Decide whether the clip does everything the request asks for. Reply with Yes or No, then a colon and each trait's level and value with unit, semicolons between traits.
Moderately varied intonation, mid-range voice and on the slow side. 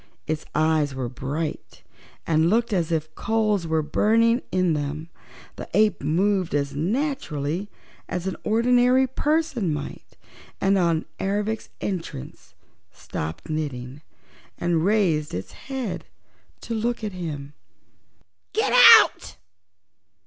No: wide, 6.1 semitones; medium, 175 Hz; slow, 115 wpm